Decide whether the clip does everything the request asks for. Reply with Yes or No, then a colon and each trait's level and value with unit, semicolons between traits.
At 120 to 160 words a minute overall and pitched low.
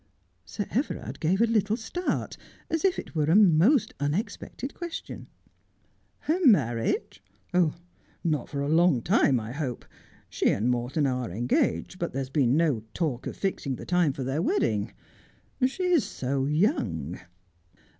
No: average, 155 wpm; medium, 160 Hz